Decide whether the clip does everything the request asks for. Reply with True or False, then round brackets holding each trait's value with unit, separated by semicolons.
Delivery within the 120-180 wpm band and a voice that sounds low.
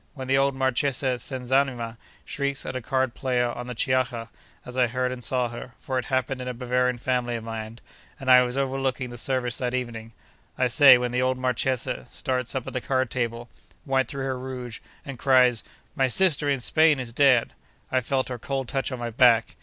False (200 wpm; 125 Hz)